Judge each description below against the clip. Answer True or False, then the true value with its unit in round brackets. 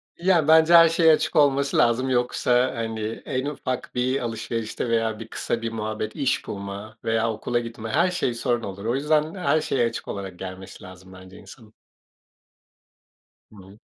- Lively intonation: False (4.2 semitones)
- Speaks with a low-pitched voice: True (115 Hz)